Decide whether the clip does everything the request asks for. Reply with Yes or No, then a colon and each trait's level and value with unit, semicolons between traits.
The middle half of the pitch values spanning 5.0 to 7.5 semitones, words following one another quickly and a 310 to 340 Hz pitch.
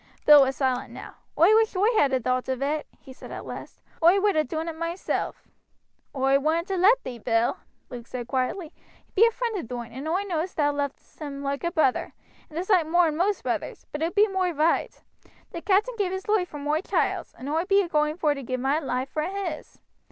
Yes: average, 5.3 semitones; fast, 225 wpm; very high, 315 Hz